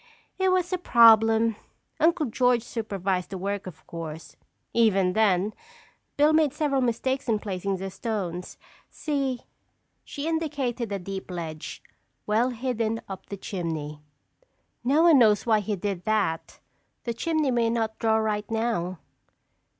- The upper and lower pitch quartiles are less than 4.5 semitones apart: No, average, 4.9 semitones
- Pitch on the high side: Yes, high, 220 Hz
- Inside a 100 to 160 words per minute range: Yes, average, 140 wpm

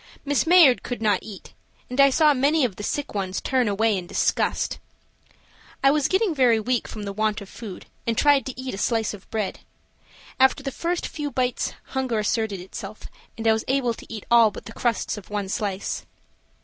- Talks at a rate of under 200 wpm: No, fast, 205 wpm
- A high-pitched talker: Yes, high, 230 Hz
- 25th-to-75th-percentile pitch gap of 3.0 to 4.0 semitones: No, average, 4.4 semitones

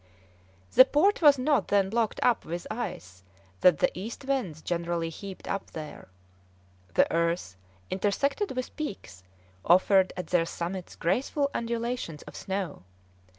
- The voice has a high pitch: Yes, high, 195 Hz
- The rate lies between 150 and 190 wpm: No, slow, 135 wpm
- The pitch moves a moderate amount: No, wide, 6.7 semitones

